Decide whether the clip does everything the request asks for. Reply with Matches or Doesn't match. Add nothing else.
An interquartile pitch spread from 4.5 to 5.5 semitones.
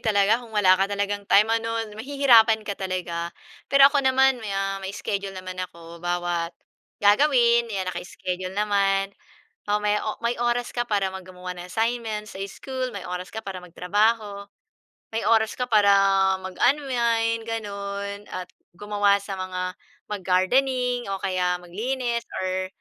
Doesn't match